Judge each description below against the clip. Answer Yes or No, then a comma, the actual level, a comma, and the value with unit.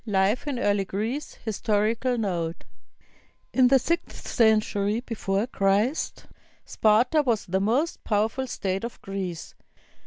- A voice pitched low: No, high, 215 Hz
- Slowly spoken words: Yes, slow, 125 wpm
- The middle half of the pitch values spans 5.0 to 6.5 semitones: No, average, 3.9 semitones